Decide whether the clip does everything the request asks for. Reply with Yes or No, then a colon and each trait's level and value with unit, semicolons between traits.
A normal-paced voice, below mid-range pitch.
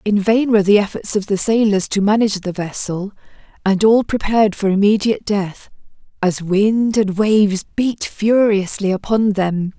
No: average, 160 wpm; high, 205 Hz